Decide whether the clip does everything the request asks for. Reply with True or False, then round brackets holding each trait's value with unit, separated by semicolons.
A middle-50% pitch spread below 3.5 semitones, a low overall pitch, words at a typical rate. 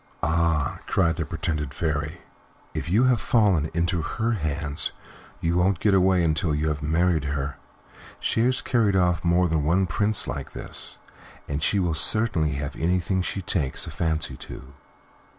False (3.8 semitones; 85 Hz; 165 wpm)